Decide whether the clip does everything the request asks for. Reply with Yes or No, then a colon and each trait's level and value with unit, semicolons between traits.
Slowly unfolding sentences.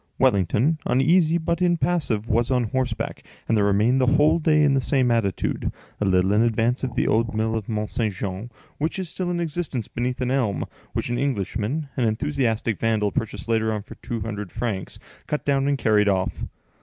No: average, 195 wpm